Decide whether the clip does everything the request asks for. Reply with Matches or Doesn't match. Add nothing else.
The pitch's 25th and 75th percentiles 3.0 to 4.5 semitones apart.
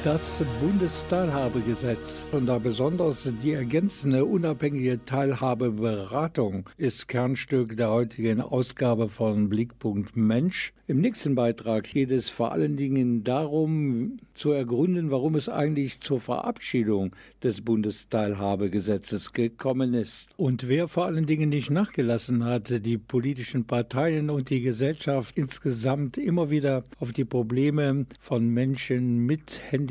Matches